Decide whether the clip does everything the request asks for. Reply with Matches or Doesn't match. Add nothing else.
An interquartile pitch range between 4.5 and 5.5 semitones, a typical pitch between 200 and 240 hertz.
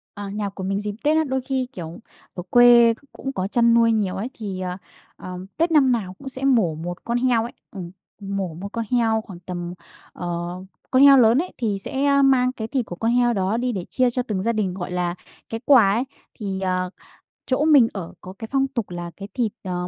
Matches